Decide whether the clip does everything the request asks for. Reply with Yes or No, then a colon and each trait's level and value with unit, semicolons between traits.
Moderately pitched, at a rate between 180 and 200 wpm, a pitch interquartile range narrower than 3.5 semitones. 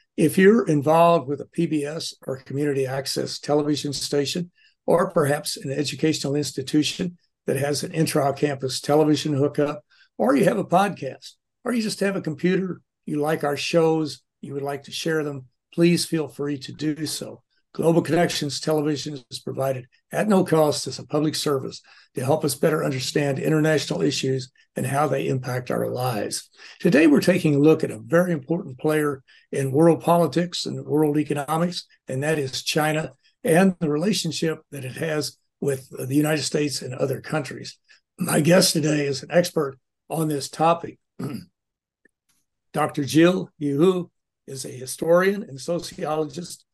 No: medium, 150 Hz; average, 160 wpm; average, 2.9 semitones